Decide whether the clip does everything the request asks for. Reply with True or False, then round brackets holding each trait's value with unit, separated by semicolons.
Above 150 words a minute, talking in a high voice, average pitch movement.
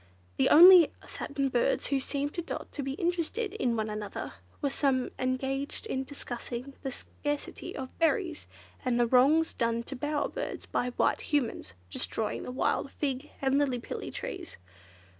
True (160 wpm; 275 Hz; 3.5 semitones)